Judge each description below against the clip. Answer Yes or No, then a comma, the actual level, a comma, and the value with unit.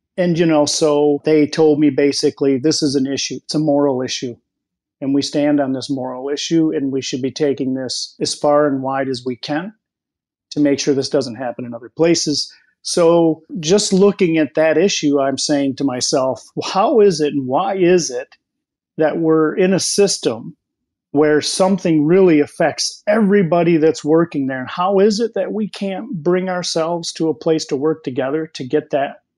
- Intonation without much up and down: No, average, 3.8 semitones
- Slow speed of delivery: No, average, 190 wpm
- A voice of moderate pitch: Yes, medium, 150 Hz